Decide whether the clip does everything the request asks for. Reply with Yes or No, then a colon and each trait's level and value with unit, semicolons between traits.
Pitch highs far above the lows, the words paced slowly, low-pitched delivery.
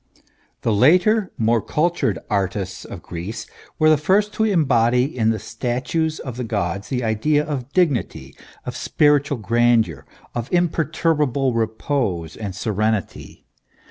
Yes: wide, 5.7 semitones; slow, 130 wpm; low, 125 Hz